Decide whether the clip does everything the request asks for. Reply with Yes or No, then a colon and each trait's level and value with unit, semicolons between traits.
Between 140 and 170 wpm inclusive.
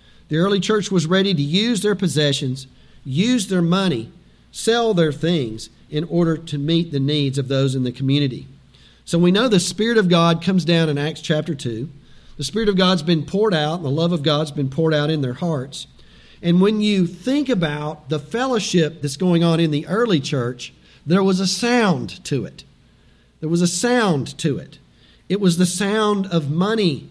No: average, 195 wpm